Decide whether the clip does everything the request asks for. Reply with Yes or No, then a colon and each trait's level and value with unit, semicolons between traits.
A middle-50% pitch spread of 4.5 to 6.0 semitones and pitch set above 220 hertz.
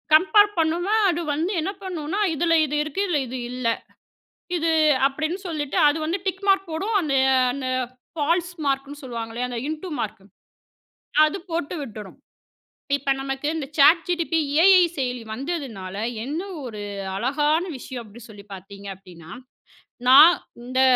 Yes: wide, 5.4 semitones; very high, 295 Hz